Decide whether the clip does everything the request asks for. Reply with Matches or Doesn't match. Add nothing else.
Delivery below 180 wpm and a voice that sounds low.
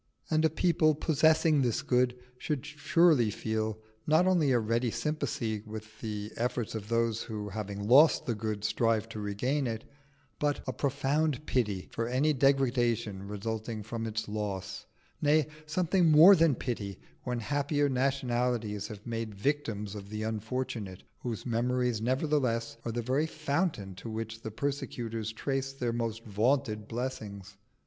Matches